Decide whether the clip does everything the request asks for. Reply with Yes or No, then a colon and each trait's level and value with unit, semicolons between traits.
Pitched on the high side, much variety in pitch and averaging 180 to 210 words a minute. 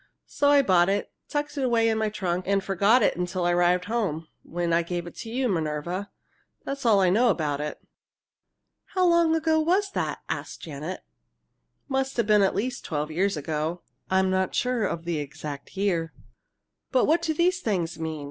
Yes: high, 195 Hz; wide, 6.8 semitones; average, 190 wpm